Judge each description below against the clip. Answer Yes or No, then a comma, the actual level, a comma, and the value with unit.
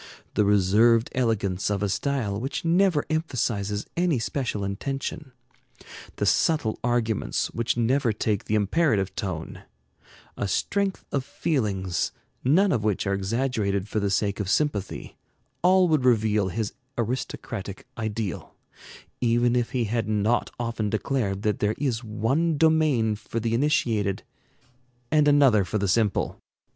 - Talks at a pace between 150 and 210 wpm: No, slow, 135 wpm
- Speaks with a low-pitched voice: Yes, low, 115 Hz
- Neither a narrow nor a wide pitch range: Yes, average, 4.9 semitones